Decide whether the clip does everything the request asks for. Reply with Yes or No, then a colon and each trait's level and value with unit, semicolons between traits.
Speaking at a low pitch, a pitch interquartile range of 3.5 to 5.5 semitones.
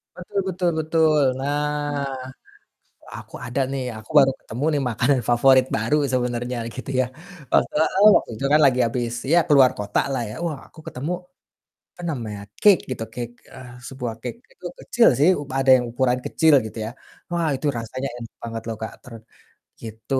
Yes: low, 130 Hz; average, 4.0 semitones